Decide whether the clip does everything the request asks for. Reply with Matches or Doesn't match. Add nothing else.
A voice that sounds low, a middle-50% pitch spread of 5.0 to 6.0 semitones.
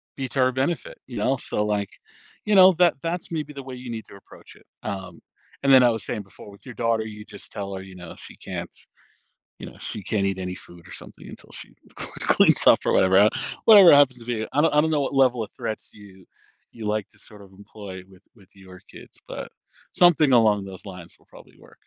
Matches